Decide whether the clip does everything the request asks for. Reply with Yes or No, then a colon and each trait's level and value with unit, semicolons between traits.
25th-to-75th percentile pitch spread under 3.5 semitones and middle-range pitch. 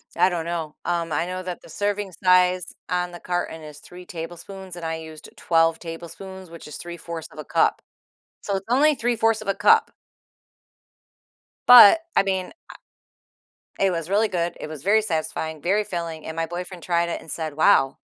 Yes: average, 2.8 semitones; medium, 175 Hz